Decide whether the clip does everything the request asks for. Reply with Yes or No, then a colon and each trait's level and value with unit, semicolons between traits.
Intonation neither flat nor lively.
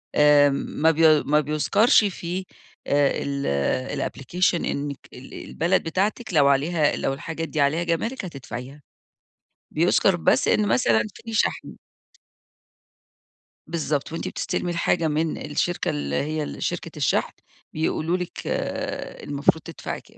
Yes: average, 3.4 semitones